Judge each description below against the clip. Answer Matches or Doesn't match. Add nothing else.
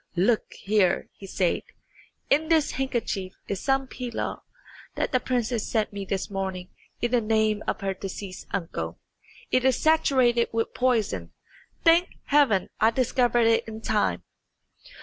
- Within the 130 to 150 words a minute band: Matches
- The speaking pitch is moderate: Doesn't match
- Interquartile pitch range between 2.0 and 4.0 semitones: Doesn't match